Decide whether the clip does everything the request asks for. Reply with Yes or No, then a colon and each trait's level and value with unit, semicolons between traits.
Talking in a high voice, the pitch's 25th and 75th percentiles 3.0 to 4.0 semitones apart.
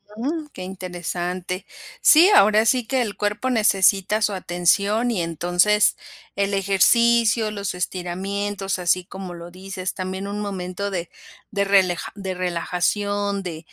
No: high, 195 Hz; narrow, 2.5 semitones